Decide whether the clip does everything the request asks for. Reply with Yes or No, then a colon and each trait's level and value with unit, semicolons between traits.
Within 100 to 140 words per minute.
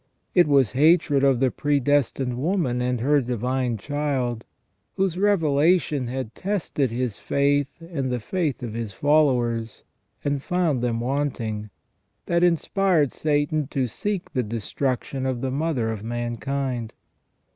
Yes: slow, 135 wpm